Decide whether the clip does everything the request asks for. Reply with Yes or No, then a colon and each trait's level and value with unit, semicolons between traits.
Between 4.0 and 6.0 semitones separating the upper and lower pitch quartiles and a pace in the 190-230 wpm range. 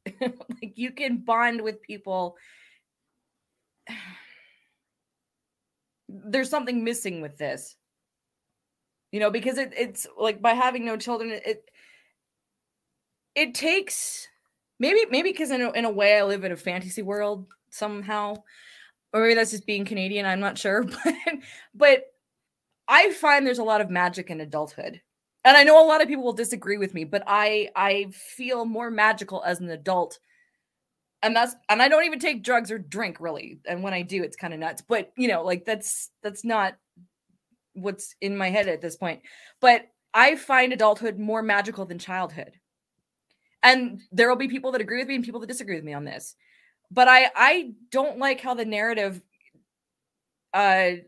No: average, 4.4 semitones; average, 170 wpm